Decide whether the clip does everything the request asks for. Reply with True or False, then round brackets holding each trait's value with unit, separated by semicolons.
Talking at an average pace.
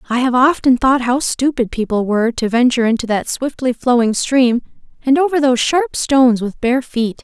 True (190 wpm)